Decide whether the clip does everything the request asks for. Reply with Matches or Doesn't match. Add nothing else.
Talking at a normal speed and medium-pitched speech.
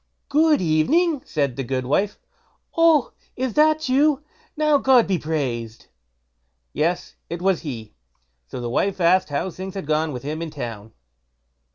Matches